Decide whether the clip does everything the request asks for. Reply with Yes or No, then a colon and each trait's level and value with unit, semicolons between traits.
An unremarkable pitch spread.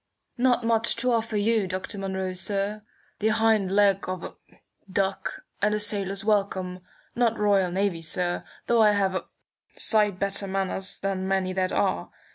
No: narrow, 2.2 semitones